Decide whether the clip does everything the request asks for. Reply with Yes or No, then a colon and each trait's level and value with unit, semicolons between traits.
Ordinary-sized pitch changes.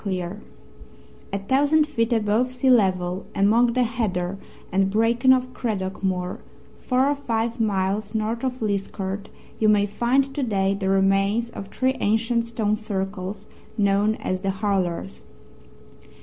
Yes: average, 3.5 semitones